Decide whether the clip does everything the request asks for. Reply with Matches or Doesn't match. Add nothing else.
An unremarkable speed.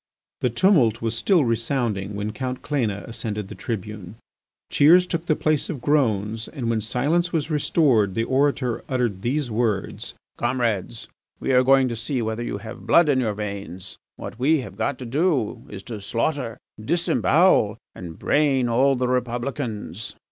Matches